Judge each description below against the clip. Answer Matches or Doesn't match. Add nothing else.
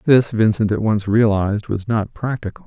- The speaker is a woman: Doesn't match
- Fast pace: Doesn't match